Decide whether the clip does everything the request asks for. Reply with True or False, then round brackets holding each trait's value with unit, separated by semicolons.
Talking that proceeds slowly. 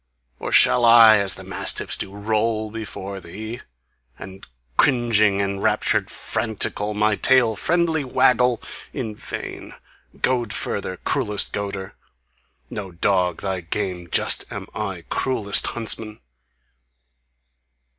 True (115 wpm)